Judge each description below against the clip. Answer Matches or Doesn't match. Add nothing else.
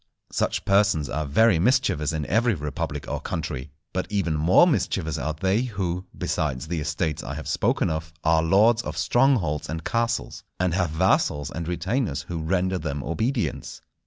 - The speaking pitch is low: Matches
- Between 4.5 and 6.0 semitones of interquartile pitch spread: Matches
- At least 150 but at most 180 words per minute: Matches